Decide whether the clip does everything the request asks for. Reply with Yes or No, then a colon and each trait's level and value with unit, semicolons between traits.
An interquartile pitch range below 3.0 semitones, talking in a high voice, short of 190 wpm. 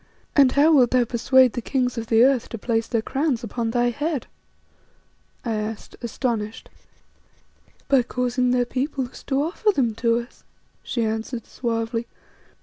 Yes: narrow, 2.5 semitones; high, 245 Hz; average, 150 wpm